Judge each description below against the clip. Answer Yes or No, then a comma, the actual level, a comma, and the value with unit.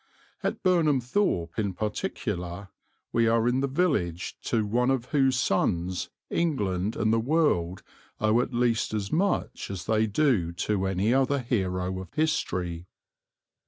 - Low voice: Yes, low, 110 Hz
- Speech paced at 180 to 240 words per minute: No, average, 145 wpm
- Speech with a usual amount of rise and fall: No, wide, 6.2 semitones